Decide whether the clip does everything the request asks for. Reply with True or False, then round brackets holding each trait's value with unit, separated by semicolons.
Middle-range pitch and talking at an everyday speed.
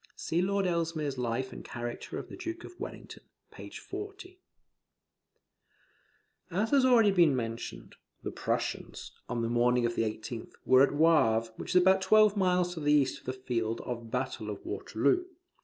True (145 Hz; 170 wpm)